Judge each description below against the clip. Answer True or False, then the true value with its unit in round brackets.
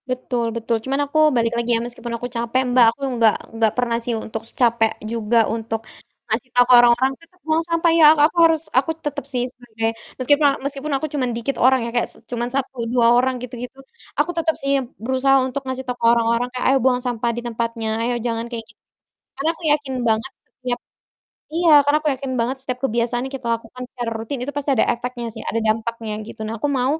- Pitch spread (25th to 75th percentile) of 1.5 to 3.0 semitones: True (2.6 semitones)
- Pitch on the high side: True (245 Hz)